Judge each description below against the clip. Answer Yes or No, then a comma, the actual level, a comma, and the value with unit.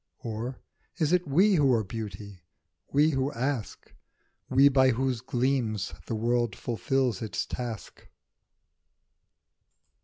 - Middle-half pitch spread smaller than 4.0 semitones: Yes, average, 3.5 semitones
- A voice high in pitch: No, low, 125 Hz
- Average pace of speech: No, slow, 115 wpm